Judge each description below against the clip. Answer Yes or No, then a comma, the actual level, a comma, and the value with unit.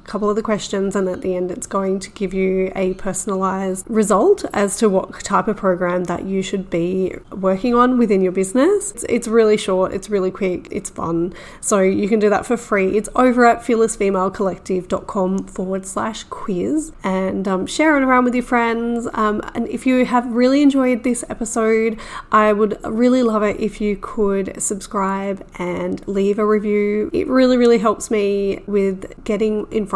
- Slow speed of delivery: No, average, 185 wpm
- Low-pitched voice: No, high, 210 Hz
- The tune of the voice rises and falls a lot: No, average, 3.3 semitones